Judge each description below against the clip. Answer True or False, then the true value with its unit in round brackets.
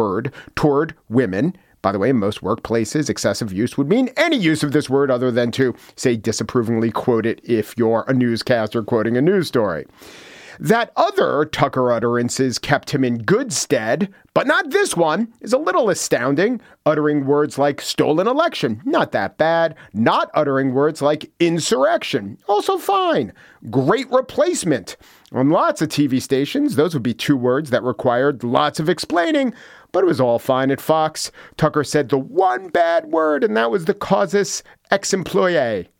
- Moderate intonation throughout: False (7.5 semitones)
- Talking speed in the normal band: True (170 wpm)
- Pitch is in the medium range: True (145 Hz)